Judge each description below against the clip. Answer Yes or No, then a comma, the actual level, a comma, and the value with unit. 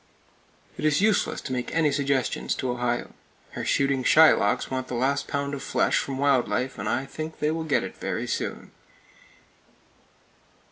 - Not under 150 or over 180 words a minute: Yes, average, 170 wpm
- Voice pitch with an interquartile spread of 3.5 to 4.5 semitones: No, narrow, 2.6 semitones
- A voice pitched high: No, medium, 140 Hz